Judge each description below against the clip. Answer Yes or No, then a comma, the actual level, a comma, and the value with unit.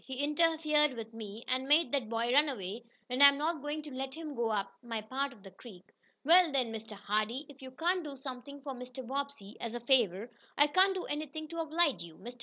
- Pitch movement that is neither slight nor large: Yes, average, 4.5 semitones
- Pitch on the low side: No, very high, 265 Hz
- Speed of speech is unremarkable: No, fast, 225 wpm